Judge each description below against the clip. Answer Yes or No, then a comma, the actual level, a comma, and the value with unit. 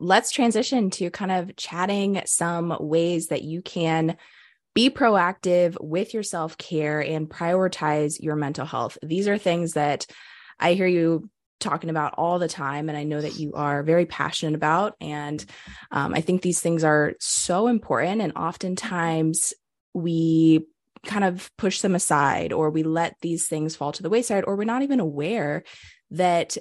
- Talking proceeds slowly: No, average, 170 wpm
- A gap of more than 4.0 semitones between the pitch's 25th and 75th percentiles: No, average, 3.1 semitones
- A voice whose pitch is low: No, medium, 170 Hz